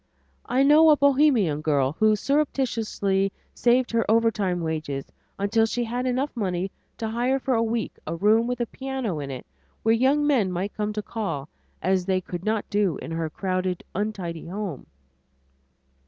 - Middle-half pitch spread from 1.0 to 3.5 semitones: No, average, 5.2 semitones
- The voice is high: Yes, high, 215 Hz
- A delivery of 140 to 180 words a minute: Yes, average, 170 wpm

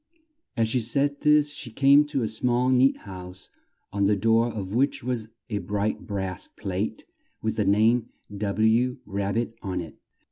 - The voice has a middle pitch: No, low, 110 Hz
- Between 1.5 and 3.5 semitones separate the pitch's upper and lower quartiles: No, average, 3.9 semitones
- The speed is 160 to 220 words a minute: Yes, average, 170 wpm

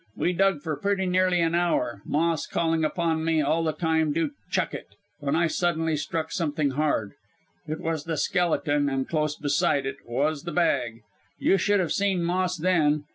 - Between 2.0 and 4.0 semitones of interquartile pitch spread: Yes, average, 2.9 semitones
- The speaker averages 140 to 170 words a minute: No, average, 185 wpm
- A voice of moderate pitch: Yes, medium, 160 Hz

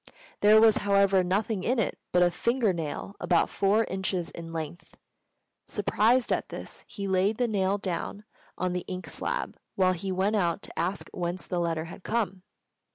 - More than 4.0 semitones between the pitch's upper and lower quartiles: No, average, 2.7 semitones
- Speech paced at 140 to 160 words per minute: No, average, 175 wpm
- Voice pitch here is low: No, high, 190 Hz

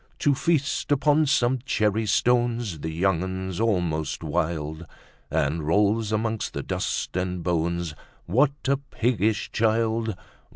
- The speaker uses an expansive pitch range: Yes, wide, 5.7 semitones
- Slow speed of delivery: Yes, slow, 125 wpm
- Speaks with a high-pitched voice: No, low, 105 Hz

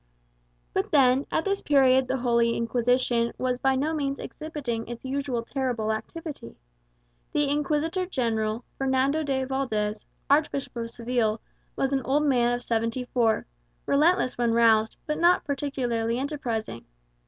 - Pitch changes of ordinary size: Yes, average, 3.3 semitones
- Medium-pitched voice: No, very high, 255 Hz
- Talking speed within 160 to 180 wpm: No, average, 140 wpm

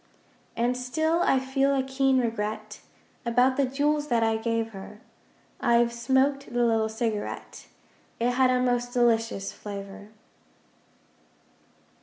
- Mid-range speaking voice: No, high, 245 Hz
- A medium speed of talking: No, slow, 125 wpm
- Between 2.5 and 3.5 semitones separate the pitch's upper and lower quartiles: Yes, average, 2.8 semitones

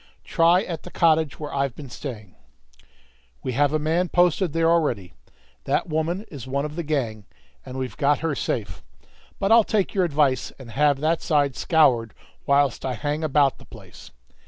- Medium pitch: Yes, medium, 150 Hz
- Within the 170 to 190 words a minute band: Yes, average, 180 wpm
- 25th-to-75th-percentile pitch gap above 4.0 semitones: No, average, 3.7 semitones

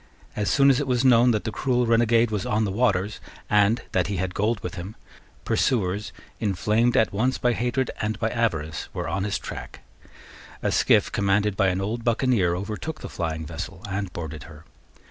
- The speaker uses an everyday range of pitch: Yes, average, 4.0 semitones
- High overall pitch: No, low, 105 Hz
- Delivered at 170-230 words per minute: Yes, average, 190 wpm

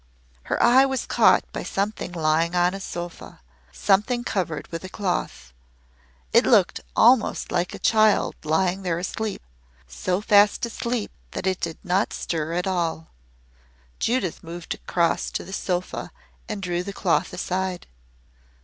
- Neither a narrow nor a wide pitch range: Yes, average, 3.3 semitones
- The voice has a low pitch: No, medium, 185 Hz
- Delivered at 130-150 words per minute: Yes, average, 145 wpm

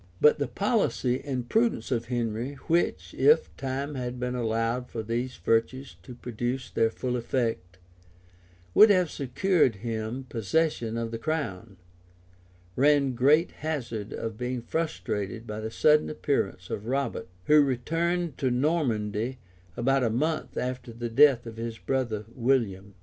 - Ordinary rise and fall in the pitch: Yes, average, 3.8 semitones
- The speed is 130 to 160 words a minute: Yes, average, 145 wpm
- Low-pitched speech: Yes, low, 125 Hz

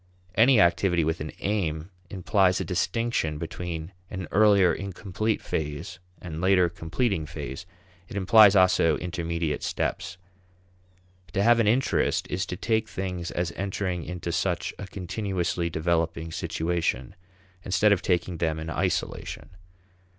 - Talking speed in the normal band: No, slow, 130 wpm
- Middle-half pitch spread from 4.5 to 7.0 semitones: No, average, 3.2 semitones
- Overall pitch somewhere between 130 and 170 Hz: No, very low, 90 Hz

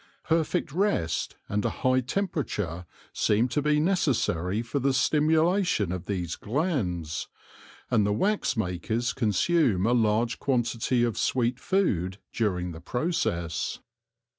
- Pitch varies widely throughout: Yes, wide, 8.3 semitones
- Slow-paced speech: Yes, slow, 130 wpm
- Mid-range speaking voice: No, low, 120 Hz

